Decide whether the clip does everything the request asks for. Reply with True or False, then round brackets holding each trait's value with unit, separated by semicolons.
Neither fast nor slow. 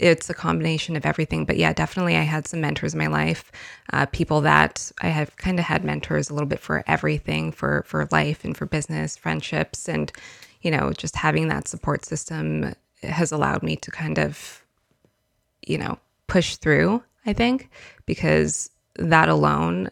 True (180 wpm)